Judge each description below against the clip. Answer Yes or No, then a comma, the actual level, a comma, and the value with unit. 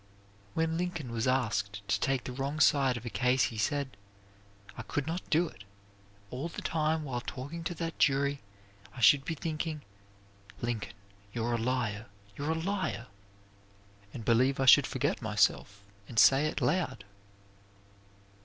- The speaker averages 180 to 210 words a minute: No, average, 165 wpm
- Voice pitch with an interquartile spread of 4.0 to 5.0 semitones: Yes, average, 4.7 semitones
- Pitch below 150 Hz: Yes, low, 135 Hz